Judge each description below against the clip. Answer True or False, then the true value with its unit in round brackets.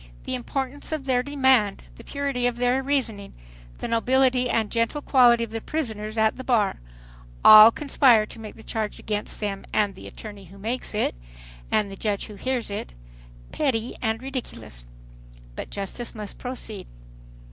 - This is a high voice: True (230 Hz)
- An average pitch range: True (3.5 semitones)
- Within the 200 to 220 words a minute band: False (165 wpm)